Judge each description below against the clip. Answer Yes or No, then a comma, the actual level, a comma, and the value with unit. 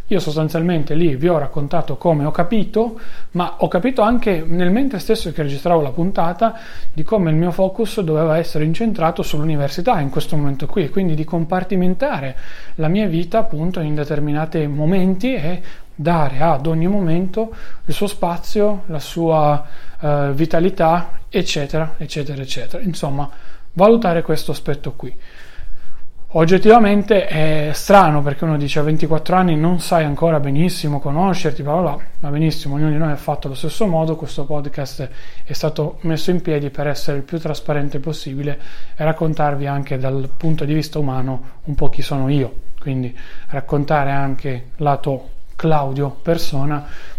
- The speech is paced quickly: No, average, 155 wpm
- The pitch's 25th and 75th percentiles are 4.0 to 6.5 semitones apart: No, average, 3.3 semitones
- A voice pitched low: No, medium, 155 Hz